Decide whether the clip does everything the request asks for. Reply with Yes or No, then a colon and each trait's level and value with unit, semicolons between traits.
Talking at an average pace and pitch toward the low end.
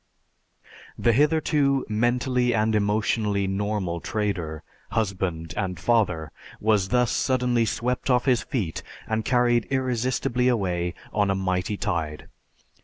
No: slow, 115 wpm; low, 110 Hz